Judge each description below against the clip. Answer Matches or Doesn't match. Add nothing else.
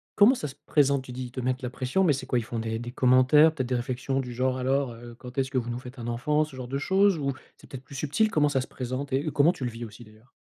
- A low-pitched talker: Matches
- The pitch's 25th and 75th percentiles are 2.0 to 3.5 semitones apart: Matches